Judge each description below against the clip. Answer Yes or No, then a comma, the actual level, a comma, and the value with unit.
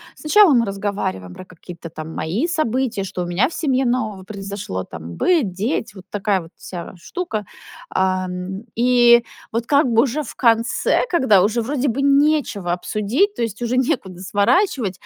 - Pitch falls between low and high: No, high, 220 Hz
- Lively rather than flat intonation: Yes, wide, 5.8 semitones